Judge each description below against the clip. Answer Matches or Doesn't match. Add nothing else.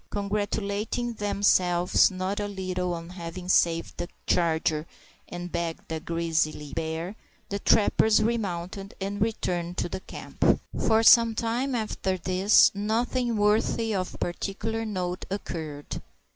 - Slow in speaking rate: Matches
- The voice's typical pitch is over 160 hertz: Matches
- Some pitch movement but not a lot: Matches